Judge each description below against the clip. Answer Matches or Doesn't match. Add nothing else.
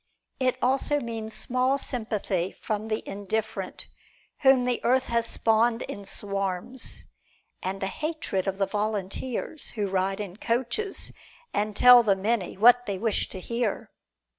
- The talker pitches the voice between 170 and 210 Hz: Doesn't match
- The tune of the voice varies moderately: Matches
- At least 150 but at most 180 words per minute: Doesn't match